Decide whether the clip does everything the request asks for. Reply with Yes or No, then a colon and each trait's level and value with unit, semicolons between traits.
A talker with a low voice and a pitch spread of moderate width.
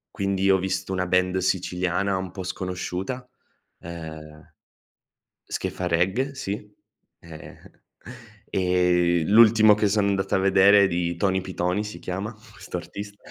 No: very low, 95 Hz; narrow, 2.0 semitones